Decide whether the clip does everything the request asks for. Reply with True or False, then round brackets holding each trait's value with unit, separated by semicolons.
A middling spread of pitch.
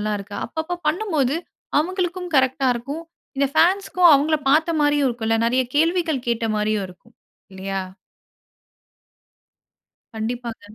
False (6.3 semitones)